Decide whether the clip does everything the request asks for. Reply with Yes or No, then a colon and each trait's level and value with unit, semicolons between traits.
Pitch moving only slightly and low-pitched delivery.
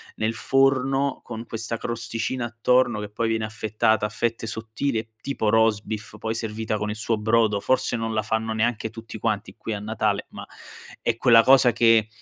Yes: narrow, 1.2 semitones; low, 115 Hz